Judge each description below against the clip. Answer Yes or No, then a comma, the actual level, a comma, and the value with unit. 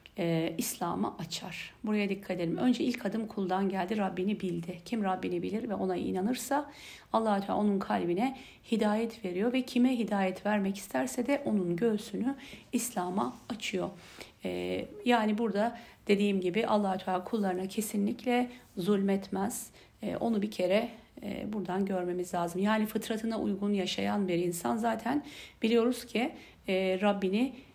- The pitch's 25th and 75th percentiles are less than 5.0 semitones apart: Yes, average, 3.8 semitones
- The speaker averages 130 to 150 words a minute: Yes, fast, 140 wpm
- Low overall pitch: No, high, 205 Hz